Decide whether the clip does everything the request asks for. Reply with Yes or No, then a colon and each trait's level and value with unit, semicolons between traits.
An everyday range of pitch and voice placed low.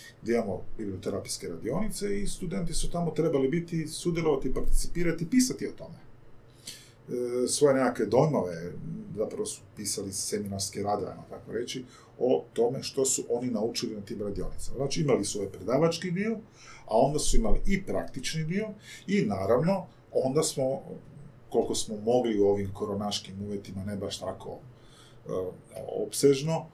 No: wide, 7.4 semitones; low, 130 Hz